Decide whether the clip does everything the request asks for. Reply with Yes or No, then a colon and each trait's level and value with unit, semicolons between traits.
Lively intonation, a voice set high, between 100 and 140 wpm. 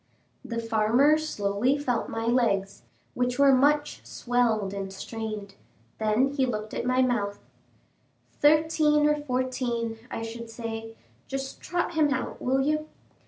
No: average, 3.9 semitones; high, 245 Hz; slow, 135 wpm